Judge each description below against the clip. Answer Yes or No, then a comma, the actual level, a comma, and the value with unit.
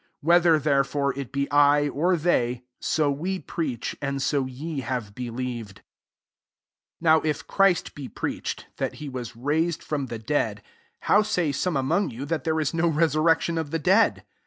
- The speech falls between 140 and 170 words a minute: No, average, 180 wpm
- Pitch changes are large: No, average, 3.8 semitones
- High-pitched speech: No, medium, 145 Hz